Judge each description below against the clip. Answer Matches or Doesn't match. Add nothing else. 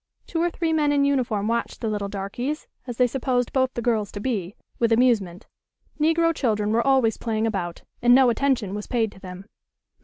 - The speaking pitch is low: Doesn't match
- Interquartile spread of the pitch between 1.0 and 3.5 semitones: Doesn't match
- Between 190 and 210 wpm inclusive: Matches